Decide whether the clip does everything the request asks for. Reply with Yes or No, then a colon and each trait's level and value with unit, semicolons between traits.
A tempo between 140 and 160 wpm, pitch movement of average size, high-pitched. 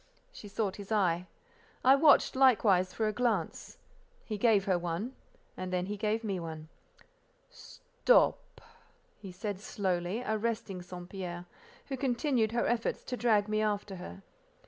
Yes: average, 145 wpm; average, 4.1 semitones; high, 210 Hz